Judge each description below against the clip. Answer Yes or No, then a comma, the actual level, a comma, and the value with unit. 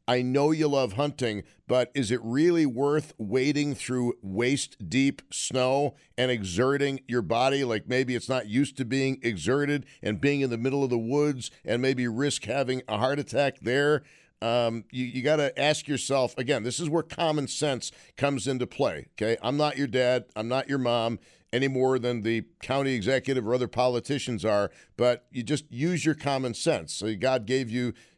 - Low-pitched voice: Yes, low, 130 Hz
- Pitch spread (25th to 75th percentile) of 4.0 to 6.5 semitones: No, average, 2.7 semitones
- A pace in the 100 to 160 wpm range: No, average, 190 wpm